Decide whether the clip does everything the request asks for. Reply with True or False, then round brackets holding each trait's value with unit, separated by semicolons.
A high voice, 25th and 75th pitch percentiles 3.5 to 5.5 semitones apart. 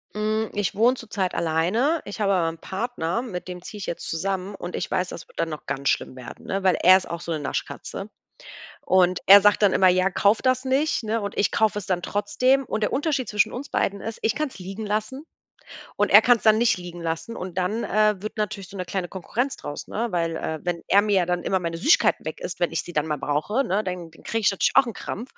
True (195 Hz; 3.9 semitones)